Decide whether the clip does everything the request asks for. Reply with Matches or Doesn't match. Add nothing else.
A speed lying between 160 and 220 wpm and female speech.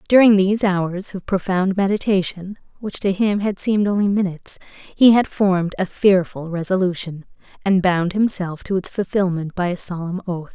Matches